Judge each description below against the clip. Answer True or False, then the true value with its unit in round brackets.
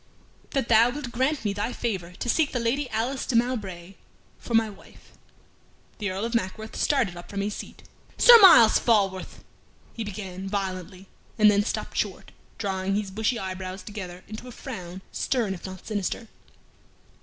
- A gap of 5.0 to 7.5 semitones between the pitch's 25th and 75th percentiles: False (3.7 semitones)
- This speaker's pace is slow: False (165 wpm)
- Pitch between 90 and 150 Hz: False (210 Hz)